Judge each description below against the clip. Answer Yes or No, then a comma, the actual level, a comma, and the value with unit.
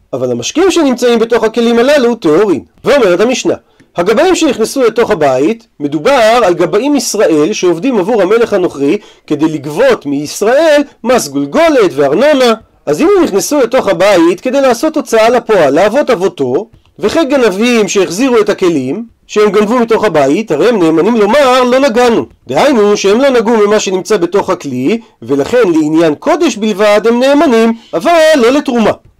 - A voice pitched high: Yes, high, 230 Hz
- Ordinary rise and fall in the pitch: No, wide, 6.4 semitones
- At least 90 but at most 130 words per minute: No, average, 145 wpm